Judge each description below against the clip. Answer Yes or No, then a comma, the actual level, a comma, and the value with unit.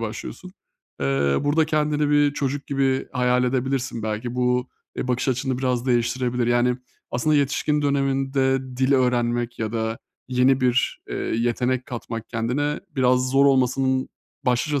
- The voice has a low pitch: Yes, low, 130 Hz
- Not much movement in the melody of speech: Yes, narrow, 2.1 semitones